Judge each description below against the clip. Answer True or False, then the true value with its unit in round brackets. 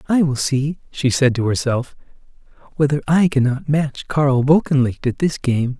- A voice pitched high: False (140 Hz)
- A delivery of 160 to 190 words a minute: True (165 wpm)